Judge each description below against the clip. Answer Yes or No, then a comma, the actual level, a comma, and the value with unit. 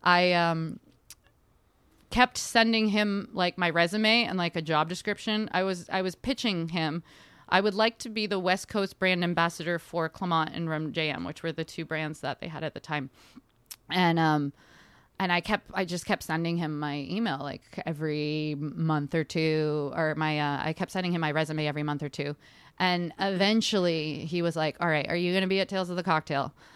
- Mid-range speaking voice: Yes, medium, 170 Hz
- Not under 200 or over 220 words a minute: Yes, fast, 205 wpm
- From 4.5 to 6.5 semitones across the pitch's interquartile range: No, average, 3.3 semitones